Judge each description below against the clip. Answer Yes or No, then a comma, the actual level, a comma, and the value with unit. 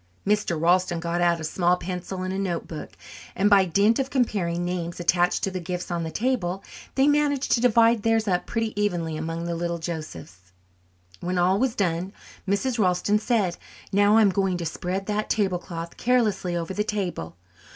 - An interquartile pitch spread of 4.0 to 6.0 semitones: No, average, 3.5 semitones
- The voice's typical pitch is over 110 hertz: Yes, medium, 185 Hz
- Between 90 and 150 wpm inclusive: No, average, 185 wpm